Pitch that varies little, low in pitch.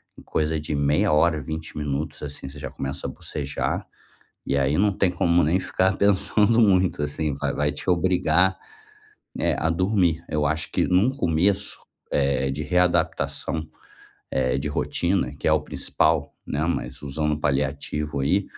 No: average, 3.8 semitones; very low, 80 Hz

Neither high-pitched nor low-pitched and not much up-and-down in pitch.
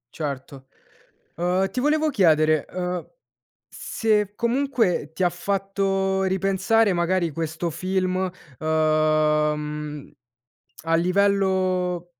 No: medium, 180 Hz; average, 3.7 semitones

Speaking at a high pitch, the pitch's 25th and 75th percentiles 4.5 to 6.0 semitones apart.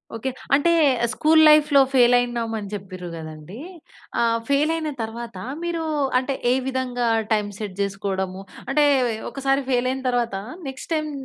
Yes: high, 245 Hz; average, 5.1 semitones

